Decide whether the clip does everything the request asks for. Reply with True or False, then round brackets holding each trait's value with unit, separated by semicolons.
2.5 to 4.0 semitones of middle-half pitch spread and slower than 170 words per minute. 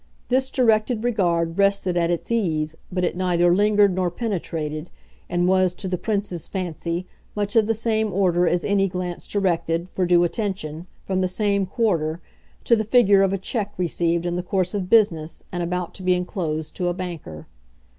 False (2.8 semitones; 185 wpm)